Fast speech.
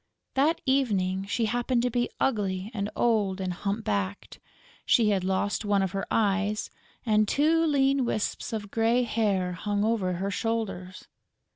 No: average, 155 wpm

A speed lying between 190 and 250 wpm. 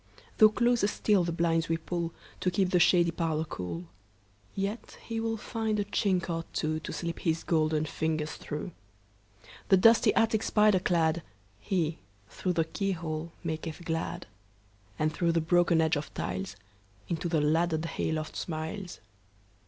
No: slow, 135 wpm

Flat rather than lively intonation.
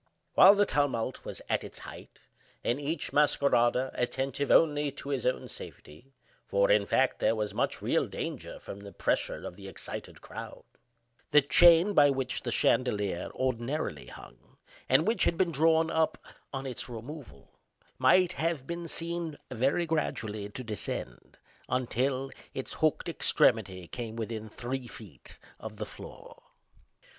No: wide, 5.4 semitones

